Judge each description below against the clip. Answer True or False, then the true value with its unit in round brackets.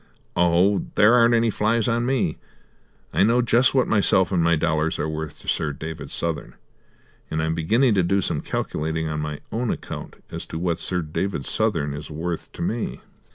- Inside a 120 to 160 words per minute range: False (185 wpm)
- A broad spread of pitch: True (6.0 semitones)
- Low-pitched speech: True (85 Hz)